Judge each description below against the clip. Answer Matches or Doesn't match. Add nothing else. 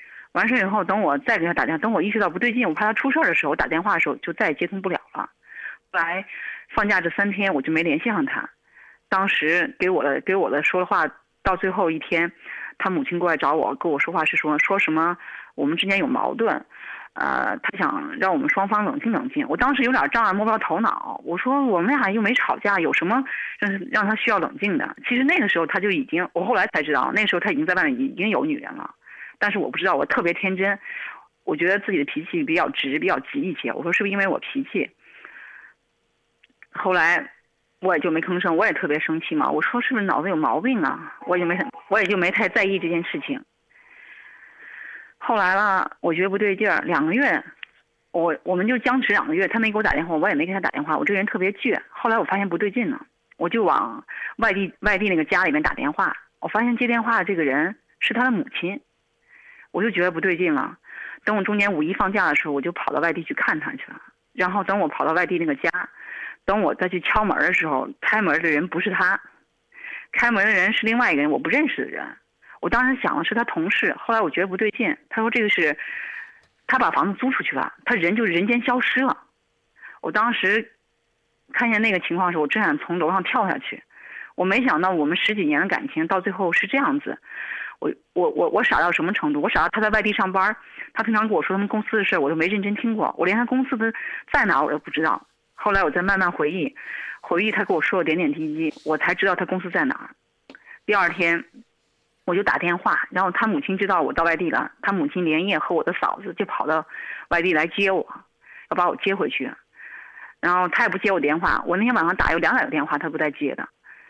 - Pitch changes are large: Matches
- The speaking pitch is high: Matches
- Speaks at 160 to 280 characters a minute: Doesn't match